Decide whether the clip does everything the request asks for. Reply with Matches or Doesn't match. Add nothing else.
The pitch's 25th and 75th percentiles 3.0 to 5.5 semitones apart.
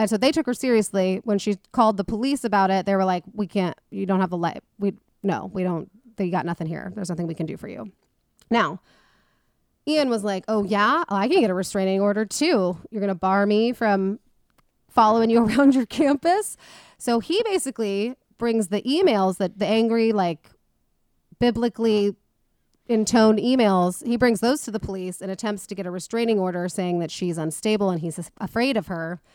Matches